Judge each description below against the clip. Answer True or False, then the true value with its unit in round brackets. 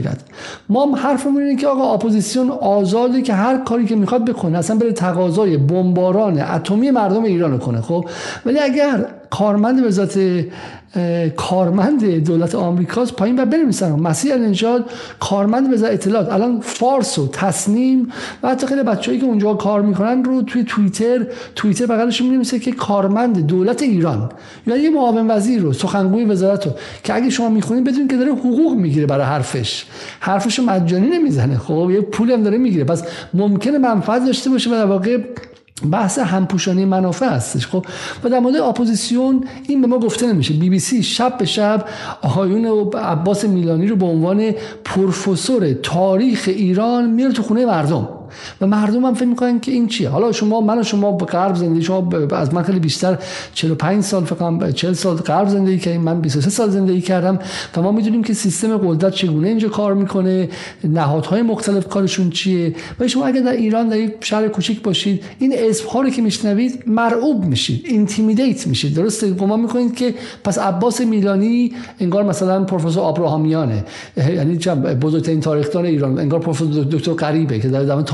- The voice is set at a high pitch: True (205 Hz)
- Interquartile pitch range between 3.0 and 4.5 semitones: False (5.1 semitones)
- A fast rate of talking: True (170 wpm)